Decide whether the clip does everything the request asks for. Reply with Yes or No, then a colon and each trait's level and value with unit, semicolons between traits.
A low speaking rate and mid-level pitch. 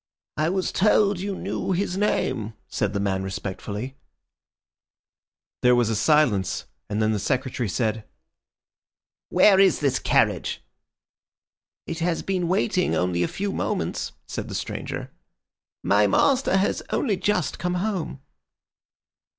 Yes: slow, 130 wpm; medium, 155 Hz